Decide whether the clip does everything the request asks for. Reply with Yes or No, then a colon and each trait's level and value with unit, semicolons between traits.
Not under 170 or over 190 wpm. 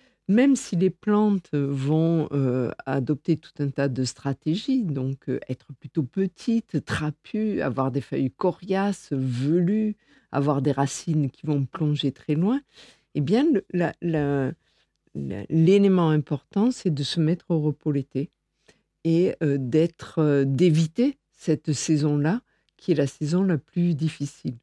No: average, 150 wpm